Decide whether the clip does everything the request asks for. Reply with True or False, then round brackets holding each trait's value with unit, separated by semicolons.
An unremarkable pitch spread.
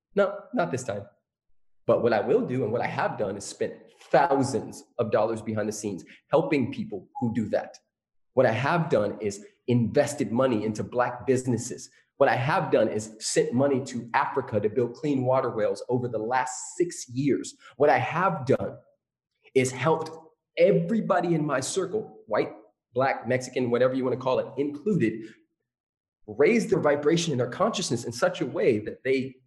False (6.2 semitones)